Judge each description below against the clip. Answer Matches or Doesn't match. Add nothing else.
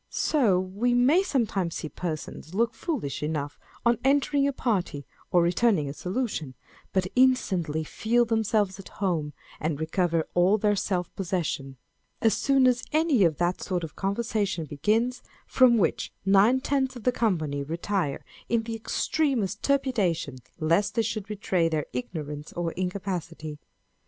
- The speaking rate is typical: Matches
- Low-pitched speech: Doesn't match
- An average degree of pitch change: Doesn't match